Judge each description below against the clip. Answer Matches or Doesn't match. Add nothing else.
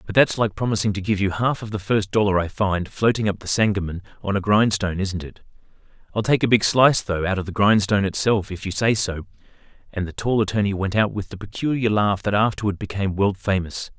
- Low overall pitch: Matches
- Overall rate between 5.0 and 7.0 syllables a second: Matches